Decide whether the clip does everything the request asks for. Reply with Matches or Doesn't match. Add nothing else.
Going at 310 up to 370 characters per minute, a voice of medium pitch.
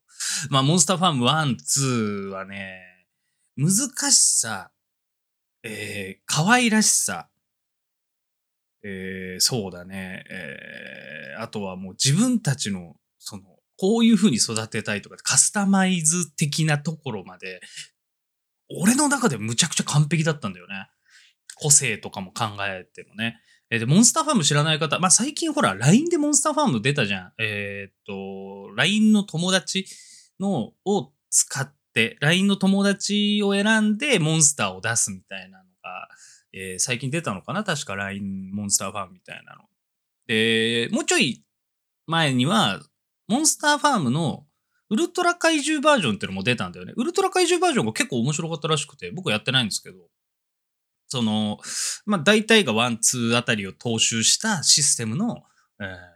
Matches